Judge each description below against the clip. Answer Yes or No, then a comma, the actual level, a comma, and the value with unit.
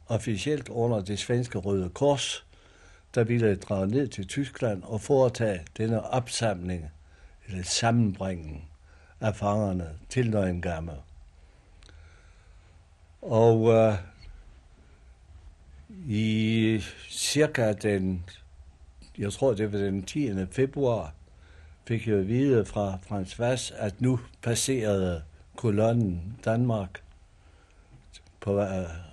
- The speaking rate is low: Yes, slow, 95 wpm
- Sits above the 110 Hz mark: No, low, 100 Hz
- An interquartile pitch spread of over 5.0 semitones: Yes, wide, 5.6 semitones